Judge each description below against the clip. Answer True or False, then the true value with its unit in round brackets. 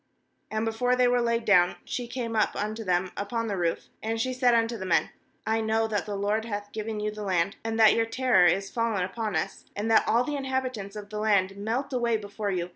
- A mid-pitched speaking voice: False (220 Hz)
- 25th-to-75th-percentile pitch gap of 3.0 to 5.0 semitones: False (2.5 semitones)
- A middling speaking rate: False (235 wpm)